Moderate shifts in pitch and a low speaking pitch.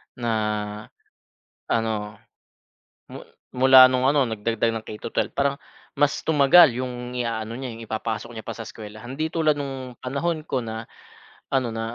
Yes: average, 3.4 semitones; low, 125 Hz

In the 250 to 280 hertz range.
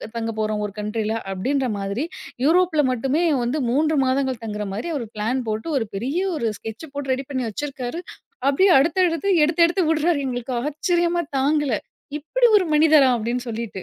Yes: very high, 270 Hz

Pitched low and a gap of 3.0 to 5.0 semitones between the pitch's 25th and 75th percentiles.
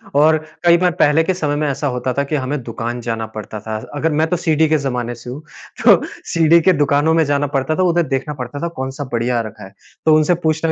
No: medium, 145 Hz; average, 4.2 semitones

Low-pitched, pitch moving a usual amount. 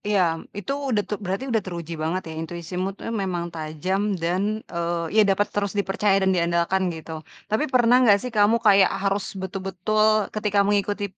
No: high, 190 Hz; average, 3.1 semitones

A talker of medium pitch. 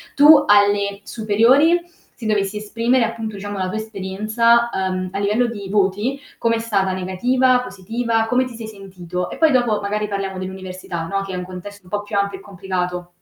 No: high, 205 Hz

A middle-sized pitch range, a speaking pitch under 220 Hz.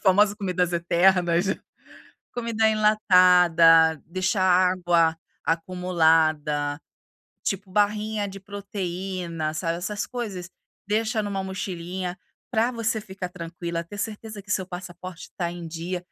Yes: average, 3.2 semitones; medium, 185 Hz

